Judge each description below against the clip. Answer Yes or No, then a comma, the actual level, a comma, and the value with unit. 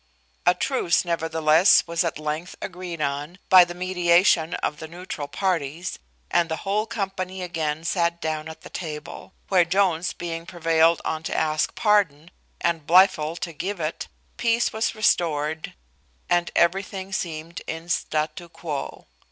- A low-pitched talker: No, medium, 170 Hz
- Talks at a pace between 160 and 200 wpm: No, average, 145 wpm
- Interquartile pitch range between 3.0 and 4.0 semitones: No, narrow, 2.6 semitones